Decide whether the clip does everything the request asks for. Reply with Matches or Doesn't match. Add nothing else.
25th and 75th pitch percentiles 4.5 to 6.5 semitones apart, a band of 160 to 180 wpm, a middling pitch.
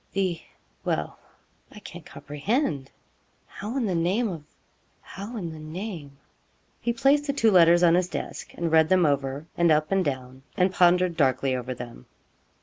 Matches